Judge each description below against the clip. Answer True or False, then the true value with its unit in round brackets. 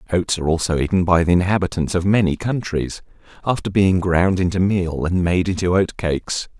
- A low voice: True (90 Hz)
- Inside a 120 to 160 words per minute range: False (180 wpm)